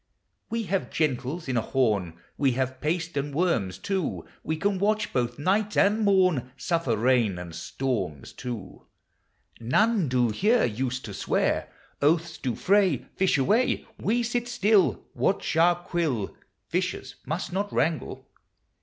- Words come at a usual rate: Yes, average, 145 wpm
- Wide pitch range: Yes, wide, 7.7 semitones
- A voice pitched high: No, medium, 160 Hz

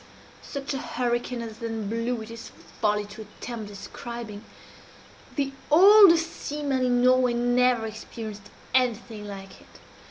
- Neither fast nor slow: No, slow, 130 wpm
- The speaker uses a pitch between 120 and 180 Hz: No, high, 235 Hz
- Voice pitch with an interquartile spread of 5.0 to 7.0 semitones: No, average, 2.8 semitones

